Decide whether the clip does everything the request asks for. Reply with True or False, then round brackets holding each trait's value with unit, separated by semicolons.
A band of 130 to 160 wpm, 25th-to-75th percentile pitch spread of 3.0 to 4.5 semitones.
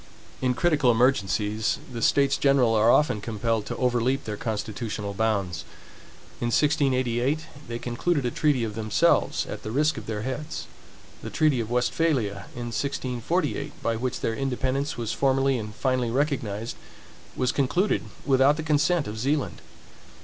True (150 wpm; 3.9 semitones)